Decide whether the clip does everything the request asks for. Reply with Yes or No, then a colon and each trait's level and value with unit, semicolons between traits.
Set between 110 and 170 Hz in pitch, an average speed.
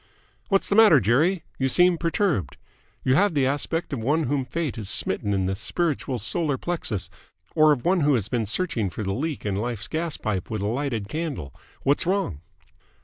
Yes: low, 135 Hz; average, 190 wpm